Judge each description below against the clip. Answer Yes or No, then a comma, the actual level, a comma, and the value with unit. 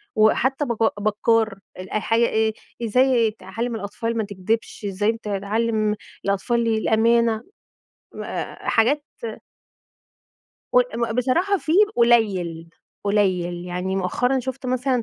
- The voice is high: Yes, high, 220 Hz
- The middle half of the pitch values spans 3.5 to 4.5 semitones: No, average, 2.9 semitones